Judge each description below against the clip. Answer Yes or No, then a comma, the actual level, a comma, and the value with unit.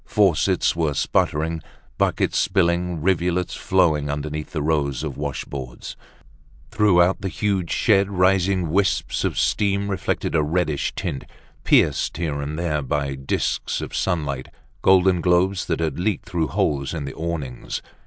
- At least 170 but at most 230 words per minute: No, average, 140 wpm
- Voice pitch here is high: No, very low, 85 Hz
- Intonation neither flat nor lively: Yes, average, 4.1 semitones